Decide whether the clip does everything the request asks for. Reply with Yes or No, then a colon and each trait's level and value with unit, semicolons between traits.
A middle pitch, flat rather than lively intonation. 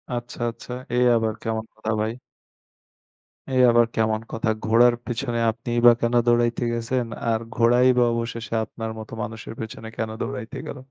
No: low, 115 Hz; narrow, 1.2 semitones